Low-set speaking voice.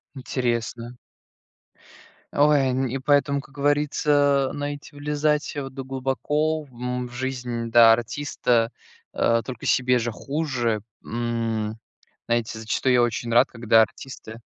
Yes: low, 125 Hz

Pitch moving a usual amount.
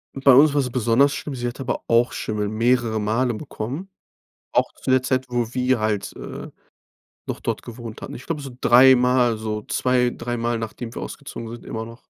No: narrow, 2.2 semitones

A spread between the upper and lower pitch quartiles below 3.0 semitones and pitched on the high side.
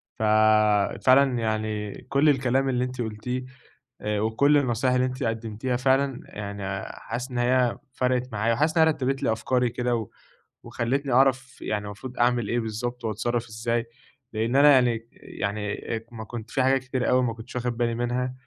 No: narrow, 2.4 semitones; low, 120 Hz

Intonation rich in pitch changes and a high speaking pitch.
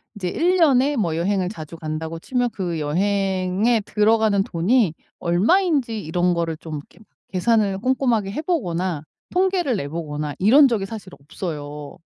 Yes: wide, 6.2 semitones; high, 195 Hz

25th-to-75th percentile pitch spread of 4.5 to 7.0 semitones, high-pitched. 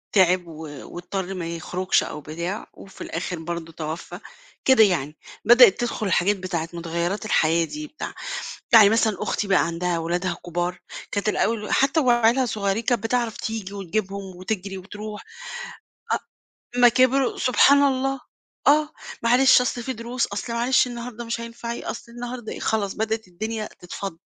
Yes: average, 5.0 semitones; high, 210 Hz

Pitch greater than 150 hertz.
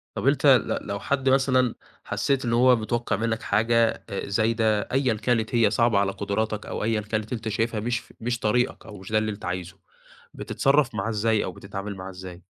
No: low, 110 Hz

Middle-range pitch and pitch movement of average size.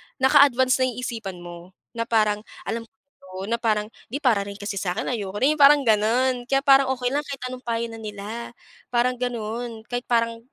No: high, 235 Hz; average, 3.0 semitones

